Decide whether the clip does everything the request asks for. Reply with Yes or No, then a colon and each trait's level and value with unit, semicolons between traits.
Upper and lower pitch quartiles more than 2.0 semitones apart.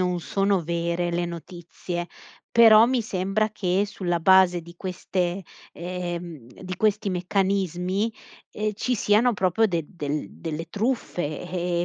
Yes: average, 2.7 semitones